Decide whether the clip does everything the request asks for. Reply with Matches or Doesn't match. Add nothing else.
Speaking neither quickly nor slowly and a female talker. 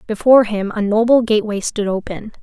Matches